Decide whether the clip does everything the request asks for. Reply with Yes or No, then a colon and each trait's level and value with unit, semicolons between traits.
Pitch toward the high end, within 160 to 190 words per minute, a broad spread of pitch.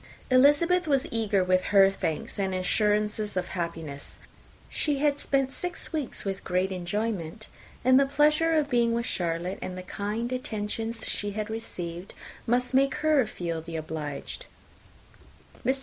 No: high, 215 Hz; average, 150 wpm; wide, 6.5 semitones